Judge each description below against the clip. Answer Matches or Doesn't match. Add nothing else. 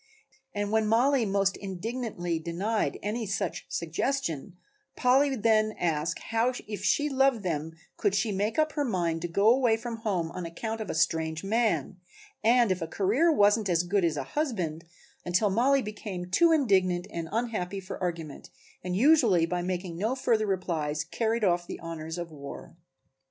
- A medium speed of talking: Matches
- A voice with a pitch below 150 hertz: Doesn't match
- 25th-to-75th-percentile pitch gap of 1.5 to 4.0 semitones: Doesn't match